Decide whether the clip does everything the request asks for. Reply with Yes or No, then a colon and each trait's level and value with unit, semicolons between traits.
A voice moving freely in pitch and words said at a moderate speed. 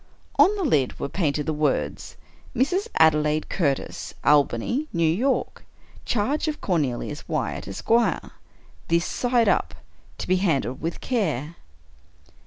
No: wide, 8.7 semitones; slow, 130 wpm